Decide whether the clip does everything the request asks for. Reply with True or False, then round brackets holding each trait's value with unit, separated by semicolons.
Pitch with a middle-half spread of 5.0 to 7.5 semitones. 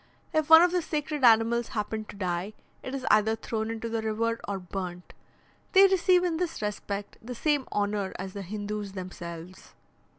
True (5.4 semitones)